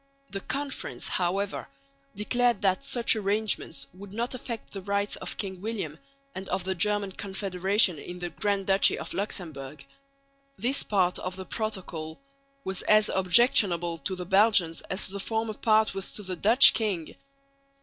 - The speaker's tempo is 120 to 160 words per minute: Yes, average, 155 wpm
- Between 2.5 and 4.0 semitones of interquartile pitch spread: Yes, average, 2.8 semitones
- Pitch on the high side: Yes, high, 195 Hz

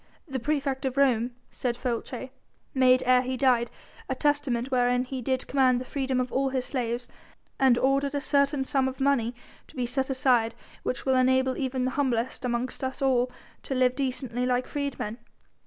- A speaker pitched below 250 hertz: No, very high, 260 Hz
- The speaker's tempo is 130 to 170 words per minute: No, average, 180 wpm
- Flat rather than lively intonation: Yes, narrow, 1.4 semitones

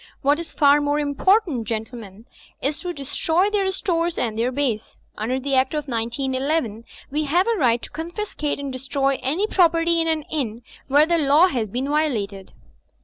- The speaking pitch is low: No, very high, 285 Hz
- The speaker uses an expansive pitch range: No, average, 4.9 semitones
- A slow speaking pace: No, average, 180 wpm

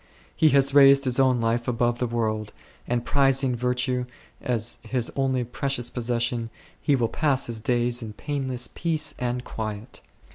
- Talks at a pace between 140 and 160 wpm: Yes, average, 155 wpm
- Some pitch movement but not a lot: No, narrow, 2.3 semitones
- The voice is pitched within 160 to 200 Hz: No, low, 125 Hz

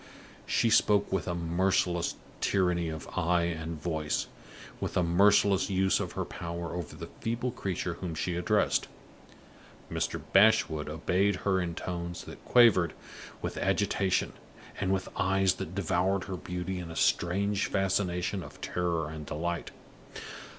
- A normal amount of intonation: No, narrow, 2.3 semitones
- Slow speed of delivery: No, average, 145 wpm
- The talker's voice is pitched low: Yes, very low, 90 Hz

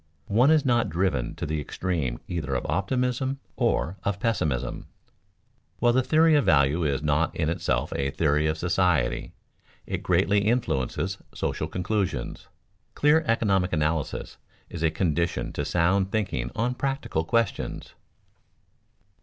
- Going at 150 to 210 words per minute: No, slow, 135 wpm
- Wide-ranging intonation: Yes, wide, 7.1 semitones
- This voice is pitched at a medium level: No, very low, 90 Hz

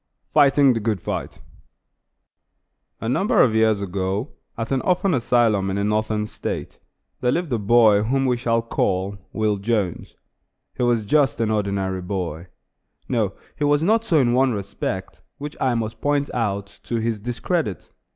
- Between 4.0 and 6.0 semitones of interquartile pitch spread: Yes, average, 4.7 semitones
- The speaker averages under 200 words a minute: Yes, average, 160 wpm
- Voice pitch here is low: Yes, low, 115 Hz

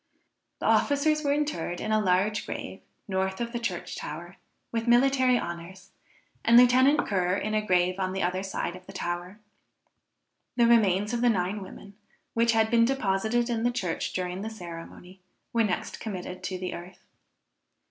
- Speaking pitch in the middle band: No, high, 205 Hz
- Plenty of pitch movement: No, average, 4.4 semitones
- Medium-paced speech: Yes, average, 170 wpm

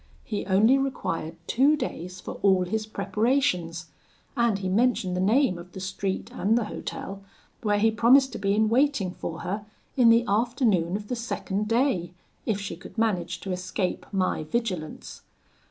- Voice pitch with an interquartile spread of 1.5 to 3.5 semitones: No, average, 4.1 semitones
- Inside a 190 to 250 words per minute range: No, average, 170 wpm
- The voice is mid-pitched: No, high, 205 Hz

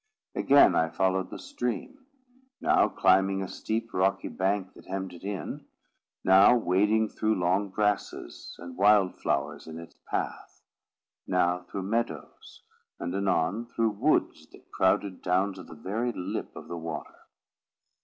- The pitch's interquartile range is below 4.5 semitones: Yes, average, 2.9 semitones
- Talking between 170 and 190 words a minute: No, average, 145 wpm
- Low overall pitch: Yes, very low, 95 Hz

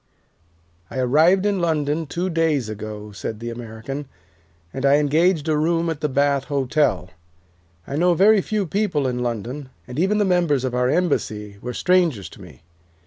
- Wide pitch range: Yes, wide, 5.7 semitones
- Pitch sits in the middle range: Yes, medium, 145 Hz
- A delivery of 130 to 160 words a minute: No, average, 175 wpm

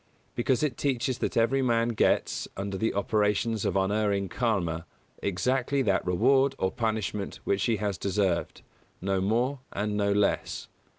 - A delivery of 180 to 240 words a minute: No, average, 150 wpm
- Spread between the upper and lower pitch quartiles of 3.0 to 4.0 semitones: Yes, average, 3.5 semitones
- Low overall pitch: Yes, low, 105 Hz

